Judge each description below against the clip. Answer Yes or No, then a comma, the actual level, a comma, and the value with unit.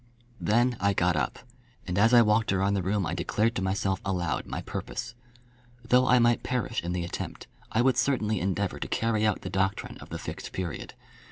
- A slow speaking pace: No, average, 200 wpm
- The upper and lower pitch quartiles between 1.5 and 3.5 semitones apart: No, average, 3.9 semitones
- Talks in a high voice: No, low, 100 Hz